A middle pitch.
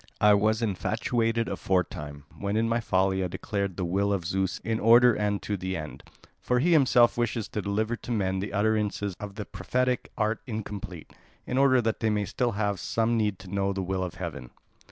No: low, 105 Hz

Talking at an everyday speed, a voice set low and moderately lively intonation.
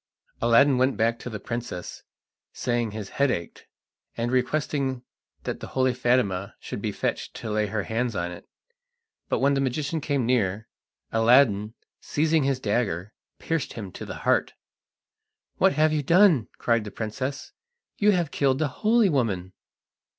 Yes: average, 160 wpm; low, 125 Hz; average, 4.5 semitones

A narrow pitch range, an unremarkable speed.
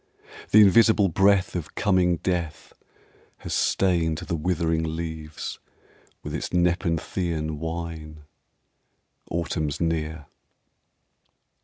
No: narrow, 2.2 semitones; slow, 90 wpm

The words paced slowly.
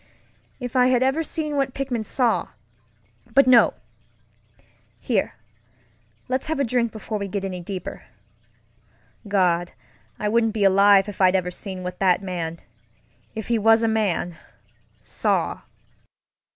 Yes: slow, 125 wpm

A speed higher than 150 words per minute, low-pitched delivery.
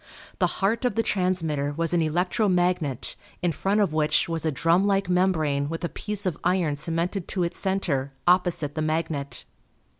No: average, 180 wpm; medium, 170 Hz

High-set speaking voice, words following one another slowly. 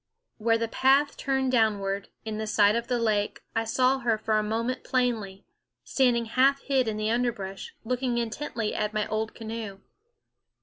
No: high, 230 Hz; average, 165 wpm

